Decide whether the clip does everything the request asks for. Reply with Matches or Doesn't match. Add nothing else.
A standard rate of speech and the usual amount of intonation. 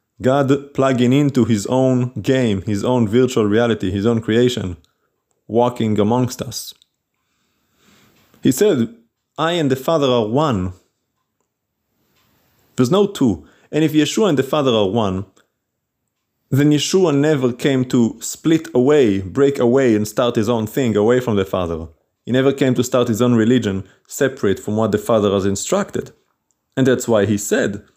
Matches